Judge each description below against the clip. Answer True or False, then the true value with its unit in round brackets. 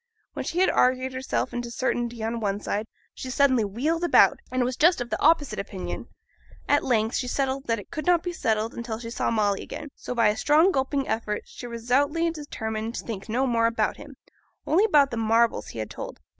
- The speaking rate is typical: False (210 wpm)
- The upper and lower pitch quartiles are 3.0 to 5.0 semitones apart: True (4.2 semitones)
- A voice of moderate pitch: False (245 Hz)